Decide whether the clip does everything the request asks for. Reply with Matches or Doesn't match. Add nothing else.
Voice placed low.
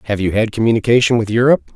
Matches